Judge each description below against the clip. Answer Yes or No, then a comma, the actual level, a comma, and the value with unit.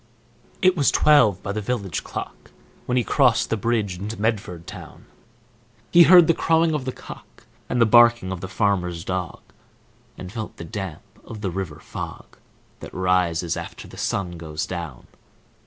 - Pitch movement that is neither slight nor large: Yes, average, 5.0 semitones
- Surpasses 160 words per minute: Yes, average, 170 wpm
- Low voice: Yes, low, 100 Hz